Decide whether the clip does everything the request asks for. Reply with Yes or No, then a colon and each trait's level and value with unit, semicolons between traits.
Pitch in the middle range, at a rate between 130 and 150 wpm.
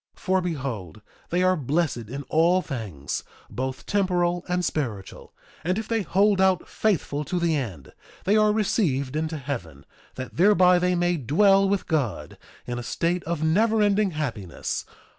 No: medium, 170 Hz; average, 160 wpm